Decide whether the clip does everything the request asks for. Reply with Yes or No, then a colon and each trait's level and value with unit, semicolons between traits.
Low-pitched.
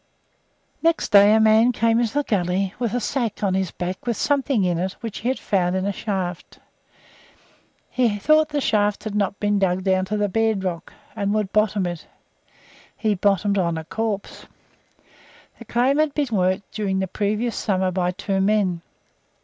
No: high, 205 Hz